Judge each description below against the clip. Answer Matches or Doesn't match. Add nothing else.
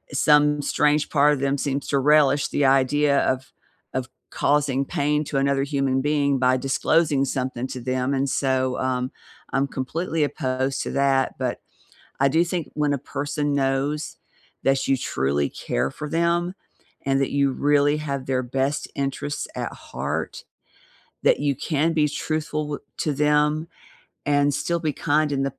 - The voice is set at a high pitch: Doesn't match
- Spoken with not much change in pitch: Matches